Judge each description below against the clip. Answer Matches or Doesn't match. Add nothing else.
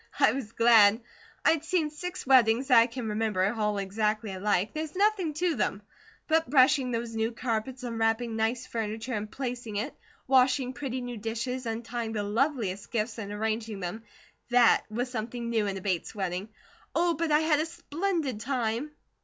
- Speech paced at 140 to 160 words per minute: Doesn't match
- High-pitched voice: Matches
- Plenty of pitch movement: Doesn't match